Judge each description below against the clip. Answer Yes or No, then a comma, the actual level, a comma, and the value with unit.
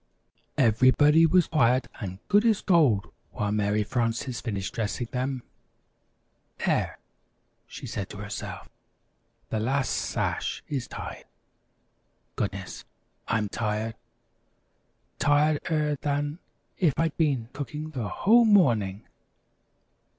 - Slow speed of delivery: Yes, slow, 105 wpm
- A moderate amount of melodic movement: No, wide, 5.7 semitones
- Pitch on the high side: No, low, 130 Hz